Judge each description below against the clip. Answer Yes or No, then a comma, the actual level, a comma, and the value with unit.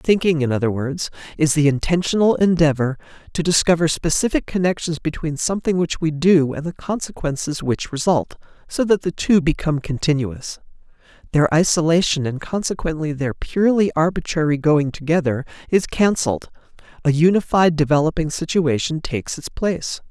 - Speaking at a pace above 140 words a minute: No, slow, 135 wpm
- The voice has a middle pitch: Yes, medium, 160 Hz